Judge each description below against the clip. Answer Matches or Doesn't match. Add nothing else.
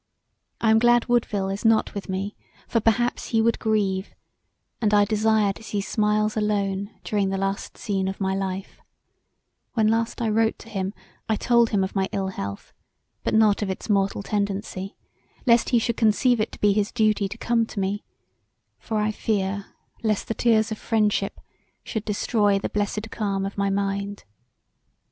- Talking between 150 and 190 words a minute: Matches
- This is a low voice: Doesn't match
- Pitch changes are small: Matches